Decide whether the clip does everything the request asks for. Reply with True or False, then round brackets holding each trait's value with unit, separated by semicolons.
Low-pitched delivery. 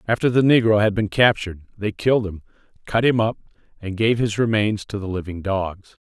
True (105 Hz)